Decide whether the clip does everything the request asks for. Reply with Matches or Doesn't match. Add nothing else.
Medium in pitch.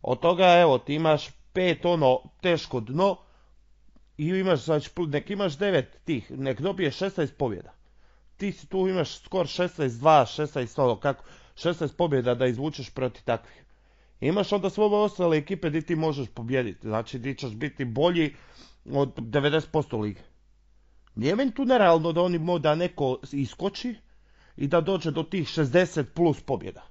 Matches